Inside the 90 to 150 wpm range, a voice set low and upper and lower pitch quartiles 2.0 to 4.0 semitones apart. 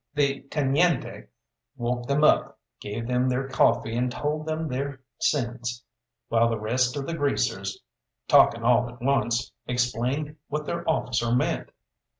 Yes: average, 145 wpm; low, 125 Hz; average, 3.2 semitones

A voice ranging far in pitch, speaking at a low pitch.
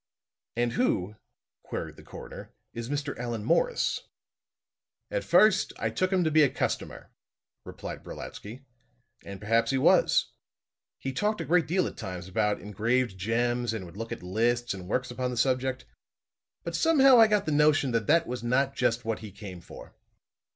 Yes: wide, 5.8 semitones; low, 120 Hz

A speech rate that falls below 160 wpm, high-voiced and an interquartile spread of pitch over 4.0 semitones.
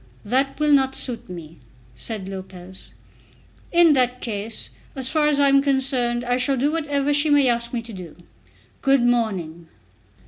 No: average, 165 wpm; very high, 250 Hz; average, 4.7 semitones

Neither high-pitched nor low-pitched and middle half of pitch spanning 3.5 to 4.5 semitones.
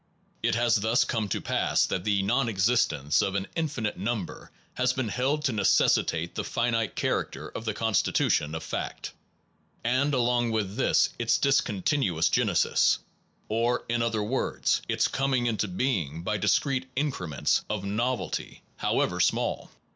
No: low, 115 Hz; average, 4.1 semitones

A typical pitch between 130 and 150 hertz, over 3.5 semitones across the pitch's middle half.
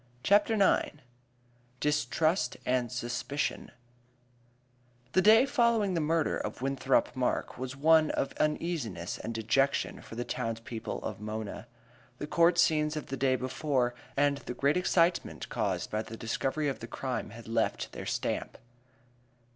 Yes: medium, 140 Hz; average, 5.1 semitones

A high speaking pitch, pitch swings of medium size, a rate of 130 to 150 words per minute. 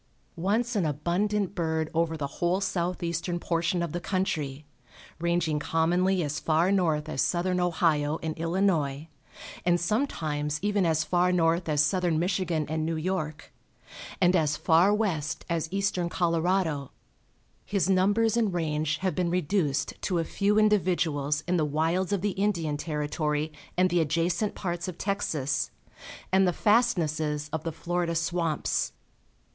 No: medium, 170 Hz; average, 3.1 semitones; average, 145 wpm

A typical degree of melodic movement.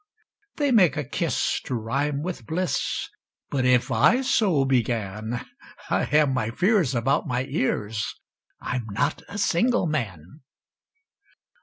No: wide, 6.3 semitones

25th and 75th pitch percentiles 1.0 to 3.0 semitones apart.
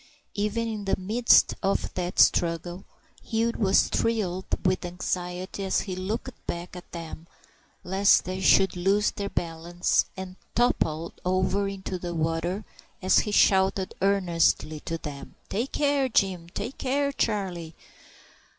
Yes: average, 2.7 semitones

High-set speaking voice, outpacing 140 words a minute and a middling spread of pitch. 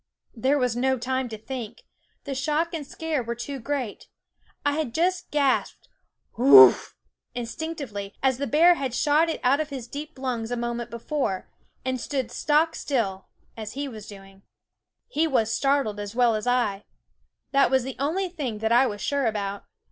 Yes: very high, 260 Hz; average, 170 wpm; average, 4.1 semitones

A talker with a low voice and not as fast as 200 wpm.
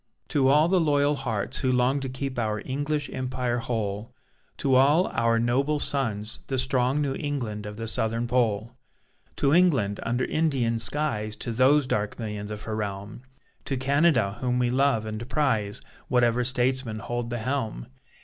Yes: low, 125 Hz; average, 165 wpm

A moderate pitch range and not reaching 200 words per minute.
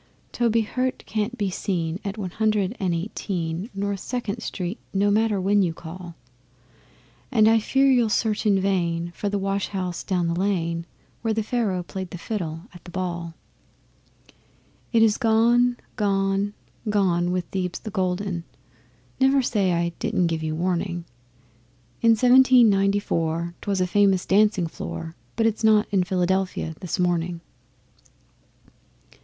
Yes: average, 3.6 semitones; average, 150 wpm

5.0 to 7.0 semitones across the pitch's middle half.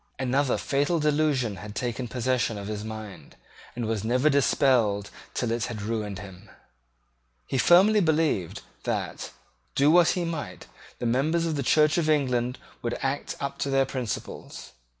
Yes: average, 5.3 semitones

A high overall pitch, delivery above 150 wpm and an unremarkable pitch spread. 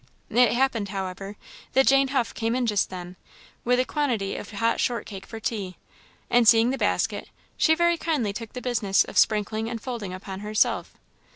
Yes: high, 225 Hz; average, 185 wpm; average, 3.8 semitones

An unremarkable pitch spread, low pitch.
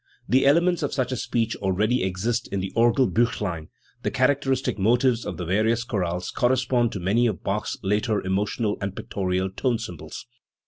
Yes: average, 4.4 semitones; low, 110 Hz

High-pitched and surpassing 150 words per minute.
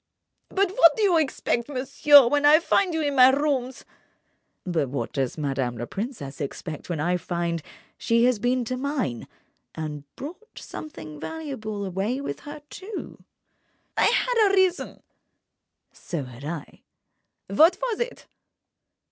No: very high, 255 Hz; average, 140 wpm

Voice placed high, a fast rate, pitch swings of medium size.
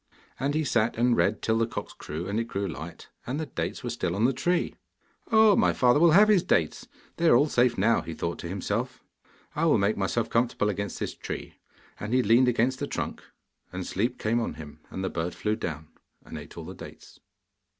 No: low, 115 Hz; fast, 225 wpm; average, 4.8 semitones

